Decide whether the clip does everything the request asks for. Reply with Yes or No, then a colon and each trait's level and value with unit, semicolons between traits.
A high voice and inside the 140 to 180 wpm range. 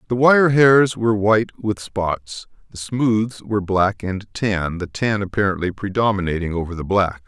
No: low, 105 Hz; average, 165 wpm